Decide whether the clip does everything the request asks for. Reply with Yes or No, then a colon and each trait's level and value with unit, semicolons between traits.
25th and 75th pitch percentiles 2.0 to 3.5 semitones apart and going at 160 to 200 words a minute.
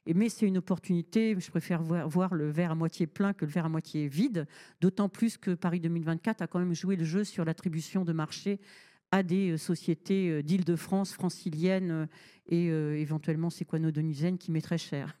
Yes: narrow, 2.6 semitones; average, 175 wpm